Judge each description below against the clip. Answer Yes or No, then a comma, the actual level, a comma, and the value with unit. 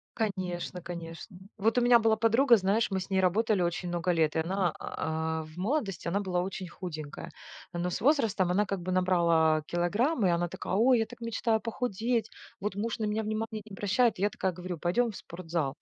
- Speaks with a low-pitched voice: No, high, 190 Hz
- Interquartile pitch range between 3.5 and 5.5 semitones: Yes, average, 4.2 semitones